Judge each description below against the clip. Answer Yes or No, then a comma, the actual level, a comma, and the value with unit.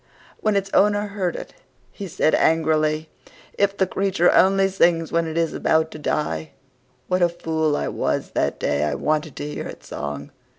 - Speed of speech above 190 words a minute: No, average, 180 wpm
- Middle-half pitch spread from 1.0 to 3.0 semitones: No, average, 3.8 semitones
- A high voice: No, medium, 165 Hz